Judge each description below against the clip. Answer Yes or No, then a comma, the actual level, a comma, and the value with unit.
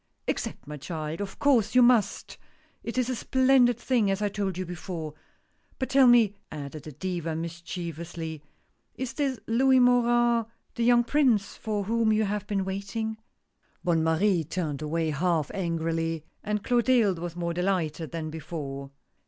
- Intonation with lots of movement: Yes, wide, 6.2 semitones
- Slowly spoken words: No, average, 165 wpm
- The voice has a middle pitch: No, high, 195 Hz